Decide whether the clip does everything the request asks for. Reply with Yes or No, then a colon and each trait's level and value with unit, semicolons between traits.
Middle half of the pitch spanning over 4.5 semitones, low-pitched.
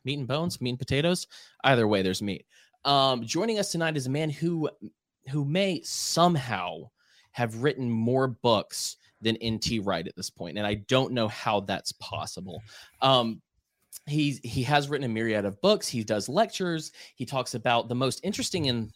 Yes: average, 5.2 semitones; low, 130 Hz